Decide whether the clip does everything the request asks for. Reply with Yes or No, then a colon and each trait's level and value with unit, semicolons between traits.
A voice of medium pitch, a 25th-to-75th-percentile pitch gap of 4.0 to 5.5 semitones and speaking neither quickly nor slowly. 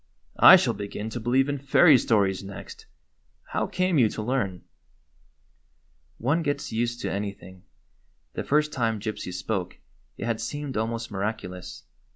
No: low, 115 Hz; average, 5.0 semitones; average, 150 wpm